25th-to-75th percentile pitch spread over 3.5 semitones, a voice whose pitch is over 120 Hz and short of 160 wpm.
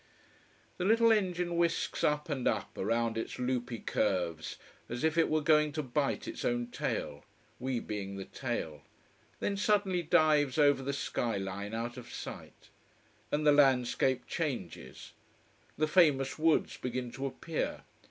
Yes: average, 4.9 semitones; low, 135 Hz; average, 150 wpm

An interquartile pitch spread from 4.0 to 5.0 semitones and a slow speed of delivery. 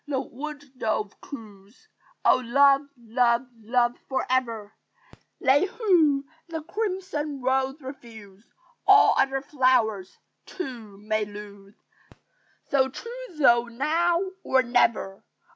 Yes: average, 4.6 semitones; slow, 110 wpm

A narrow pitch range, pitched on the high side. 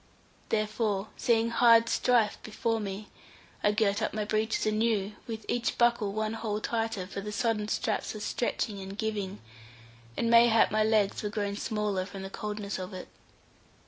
Yes: narrow, 1.8 semitones; high, 215 Hz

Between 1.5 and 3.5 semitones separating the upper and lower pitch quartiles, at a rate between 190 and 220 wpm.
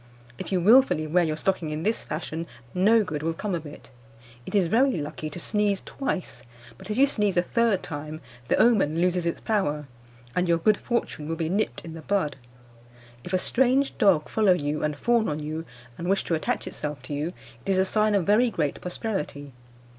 No: average, 5.3 semitones; fast, 205 wpm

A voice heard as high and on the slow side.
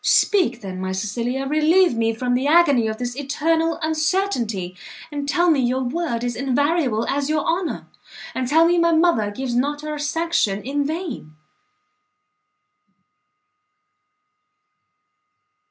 Yes: very high, 280 Hz; slow, 130 wpm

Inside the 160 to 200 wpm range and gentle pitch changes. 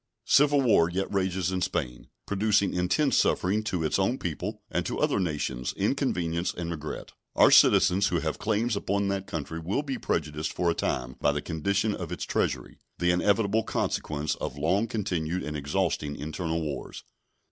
No: average, 170 wpm; average, 4.4 semitones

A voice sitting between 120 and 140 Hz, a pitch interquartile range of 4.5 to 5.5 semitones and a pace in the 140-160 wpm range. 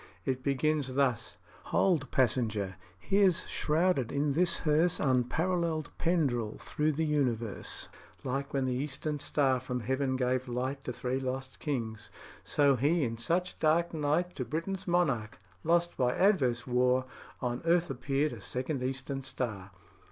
No: low, 135 Hz; average, 3.9 semitones; average, 145 wpm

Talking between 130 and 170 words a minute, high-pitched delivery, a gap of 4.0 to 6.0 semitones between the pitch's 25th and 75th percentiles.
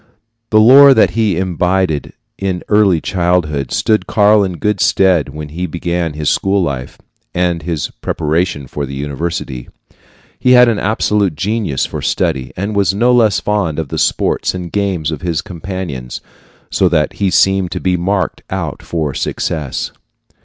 No: average, 160 wpm; very low, 90 Hz; average, 4.6 semitones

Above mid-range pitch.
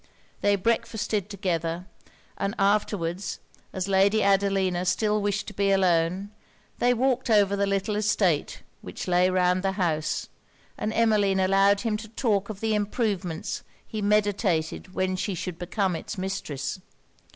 Yes: high, 195 Hz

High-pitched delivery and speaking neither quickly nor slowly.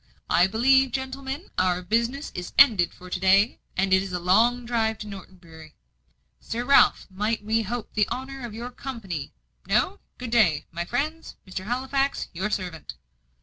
Yes: high, 220 Hz; average, 175 wpm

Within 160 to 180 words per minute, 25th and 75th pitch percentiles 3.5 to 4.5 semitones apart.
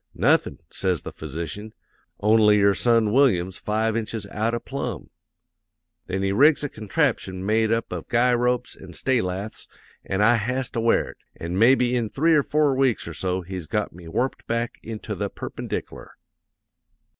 Yes: average, 170 wpm; average, 4.1 semitones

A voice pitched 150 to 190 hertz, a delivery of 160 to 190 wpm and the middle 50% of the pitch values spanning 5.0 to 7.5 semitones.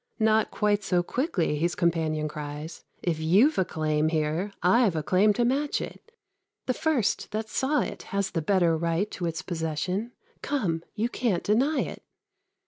Yes: medium, 185 Hz; average, 165 wpm; wide, 5.6 semitones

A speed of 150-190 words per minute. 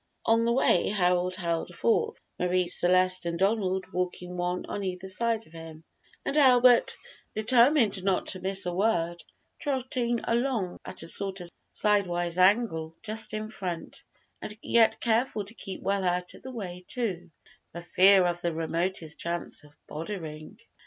Yes: average, 160 wpm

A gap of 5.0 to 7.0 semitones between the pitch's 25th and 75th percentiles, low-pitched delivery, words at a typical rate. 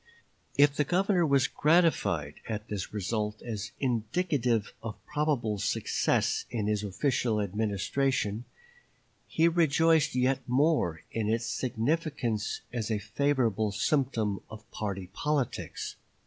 No: wide, 5.4 semitones; low, 115 Hz; slow, 115 wpm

